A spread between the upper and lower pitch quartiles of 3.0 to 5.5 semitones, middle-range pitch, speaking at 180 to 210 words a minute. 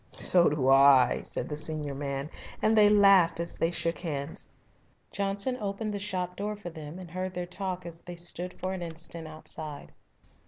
Yes: average, 3.6 semitones; medium, 175 Hz; average, 185 wpm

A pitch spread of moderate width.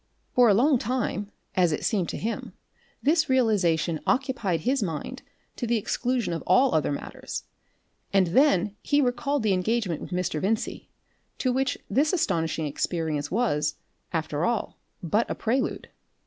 No: wide, 7.0 semitones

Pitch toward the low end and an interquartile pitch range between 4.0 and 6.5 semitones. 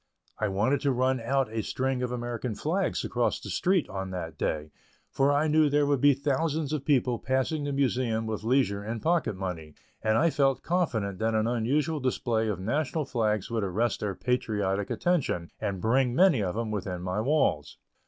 Yes: low, 120 Hz; average, 5.1 semitones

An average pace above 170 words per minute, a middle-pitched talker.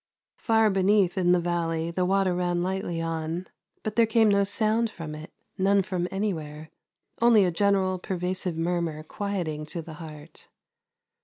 No: average, 155 wpm; medium, 180 Hz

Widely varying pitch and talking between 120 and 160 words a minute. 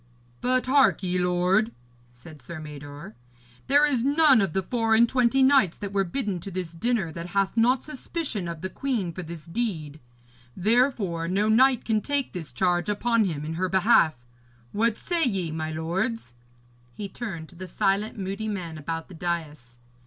No: wide, 6.0 semitones; average, 175 wpm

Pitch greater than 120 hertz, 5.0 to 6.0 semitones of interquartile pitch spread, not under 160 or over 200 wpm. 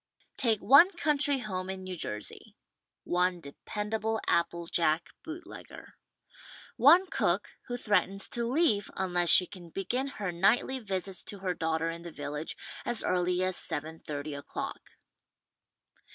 No: medium, 185 Hz; wide, 5.4 semitones; average, 150 wpm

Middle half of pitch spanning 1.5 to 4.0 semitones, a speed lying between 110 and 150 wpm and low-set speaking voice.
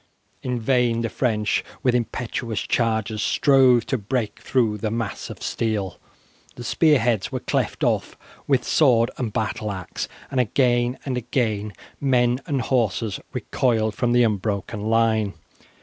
Yes: narrow, 2.5 semitones; average, 145 wpm; low, 115 Hz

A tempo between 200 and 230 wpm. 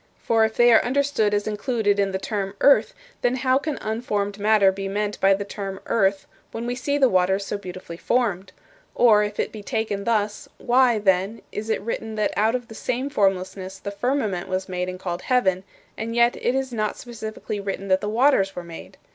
Yes: fast, 205 wpm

